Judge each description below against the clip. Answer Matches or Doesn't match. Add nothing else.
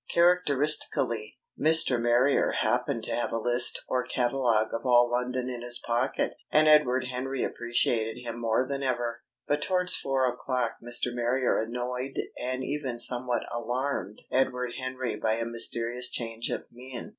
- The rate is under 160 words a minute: Matches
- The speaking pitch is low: Matches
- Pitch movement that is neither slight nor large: Doesn't match